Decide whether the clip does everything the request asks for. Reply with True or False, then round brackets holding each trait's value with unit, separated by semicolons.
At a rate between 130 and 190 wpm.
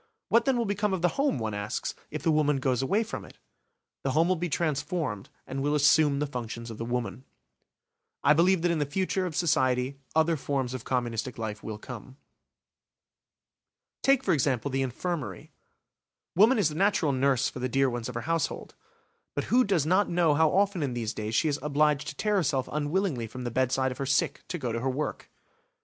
False (205 wpm)